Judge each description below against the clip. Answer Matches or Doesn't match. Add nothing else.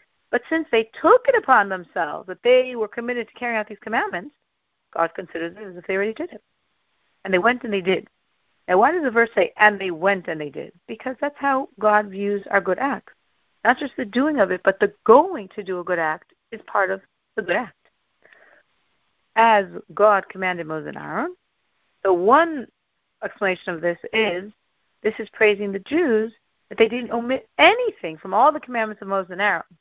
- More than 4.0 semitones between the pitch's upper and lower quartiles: Matches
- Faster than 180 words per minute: Matches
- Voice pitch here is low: Doesn't match